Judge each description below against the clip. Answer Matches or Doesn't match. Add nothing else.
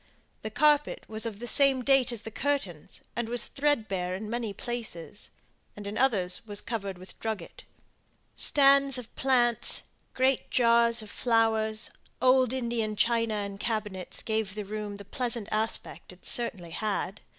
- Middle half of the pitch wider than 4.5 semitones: Doesn't match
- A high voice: Matches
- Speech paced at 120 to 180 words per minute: Matches